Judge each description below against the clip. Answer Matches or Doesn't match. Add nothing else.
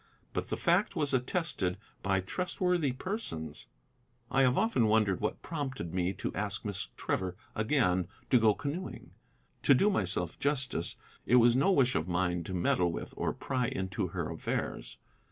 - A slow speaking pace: Doesn't match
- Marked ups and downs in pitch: Matches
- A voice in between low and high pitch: Doesn't match